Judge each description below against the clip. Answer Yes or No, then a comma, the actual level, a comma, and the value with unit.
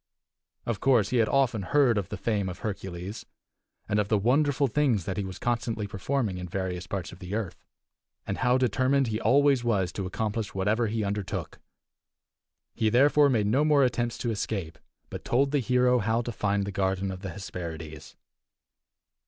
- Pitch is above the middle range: No, low, 110 Hz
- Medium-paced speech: Yes, average, 180 wpm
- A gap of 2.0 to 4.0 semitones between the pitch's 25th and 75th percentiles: No, average, 4.4 semitones